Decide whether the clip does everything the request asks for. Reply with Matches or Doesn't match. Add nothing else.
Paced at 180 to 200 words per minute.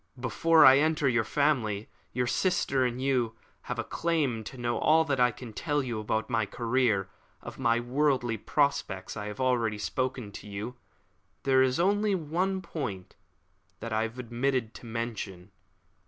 Doesn't match